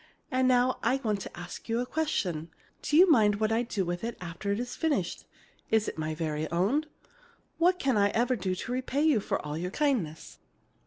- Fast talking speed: Yes, fast, 210 wpm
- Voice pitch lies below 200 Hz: No, high, 220 Hz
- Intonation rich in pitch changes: Yes, wide, 6.3 semitones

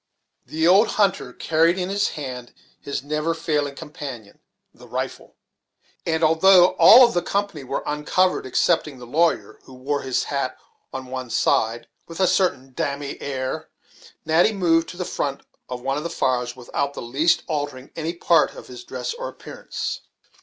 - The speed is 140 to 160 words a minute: No, average, 170 wpm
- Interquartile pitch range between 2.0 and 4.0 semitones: No, average, 4.6 semitones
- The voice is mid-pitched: Yes, medium, 150 Hz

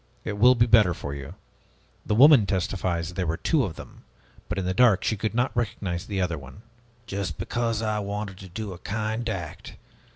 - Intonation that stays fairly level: No, average, 3.8 semitones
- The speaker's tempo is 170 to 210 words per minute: Yes, average, 200 wpm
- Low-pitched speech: Yes, low, 100 Hz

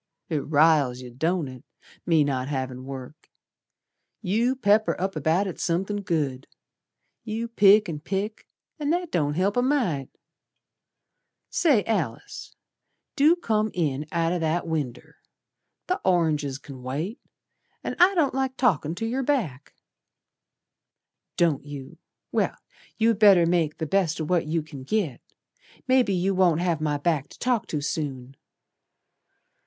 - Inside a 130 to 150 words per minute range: Yes, average, 140 wpm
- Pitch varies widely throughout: Yes, wide, 6.5 semitones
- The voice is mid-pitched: Yes, medium, 170 Hz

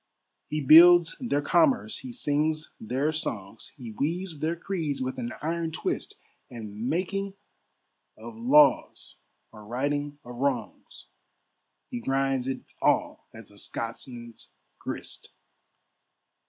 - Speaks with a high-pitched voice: No, medium, 140 Hz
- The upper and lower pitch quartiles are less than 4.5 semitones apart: No, wide, 5.4 semitones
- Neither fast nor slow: No, slow, 115 wpm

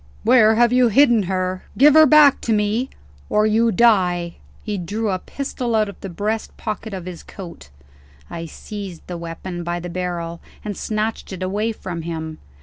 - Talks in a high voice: Yes, high, 205 Hz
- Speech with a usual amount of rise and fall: Yes, average, 4.3 semitones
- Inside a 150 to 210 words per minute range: Yes, average, 180 wpm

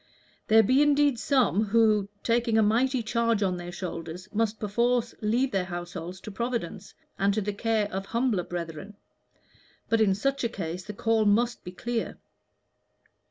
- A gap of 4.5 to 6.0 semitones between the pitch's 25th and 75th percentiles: No, average, 3.5 semitones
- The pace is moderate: Yes, average, 160 wpm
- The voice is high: Yes, high, 215 Hz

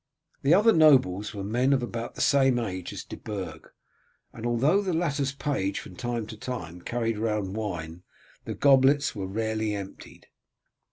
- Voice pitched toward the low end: Yes, low, 115 Hz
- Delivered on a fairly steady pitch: No, average, 5.1 semitones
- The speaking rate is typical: Yes, average, 165 wpm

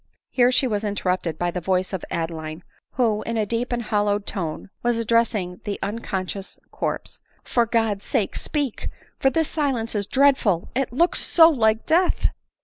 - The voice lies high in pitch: Yes, high, 220 Hz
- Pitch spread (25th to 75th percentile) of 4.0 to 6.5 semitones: Yes, average, 4.5 semitones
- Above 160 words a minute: Yes, average, 180 wpm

